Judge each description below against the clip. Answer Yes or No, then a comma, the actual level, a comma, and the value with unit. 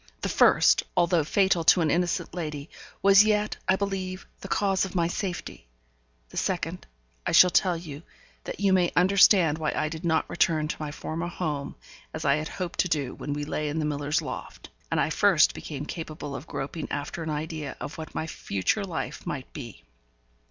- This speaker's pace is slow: No, average, 195 wpm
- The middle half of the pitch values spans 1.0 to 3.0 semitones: No, average, 3.5 semitones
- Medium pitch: Yes, medium, 160 Hz